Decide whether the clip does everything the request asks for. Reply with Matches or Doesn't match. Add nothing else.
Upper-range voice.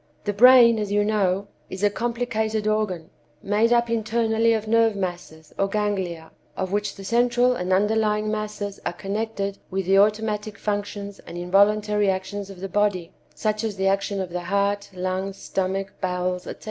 Matches